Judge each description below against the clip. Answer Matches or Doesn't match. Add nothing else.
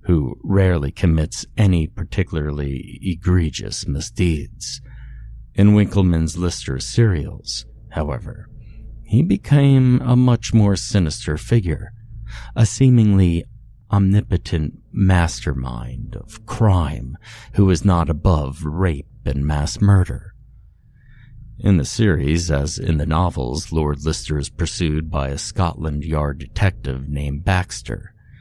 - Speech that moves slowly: Matches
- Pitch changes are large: Matches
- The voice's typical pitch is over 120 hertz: Doesn't match